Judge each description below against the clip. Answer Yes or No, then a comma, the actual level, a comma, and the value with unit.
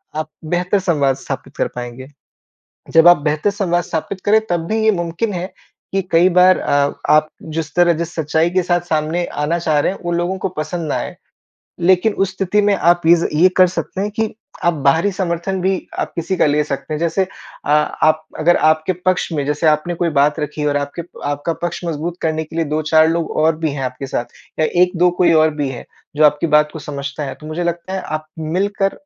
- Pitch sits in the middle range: Yes, medium, 170 Hz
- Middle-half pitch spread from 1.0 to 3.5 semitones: Yes, average, 2.8 semitones